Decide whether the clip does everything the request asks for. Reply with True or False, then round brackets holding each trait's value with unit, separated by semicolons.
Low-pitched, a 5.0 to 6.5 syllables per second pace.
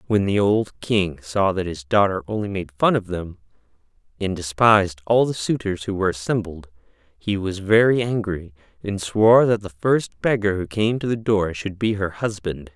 False (100 Hz; 4.8 syllables/s)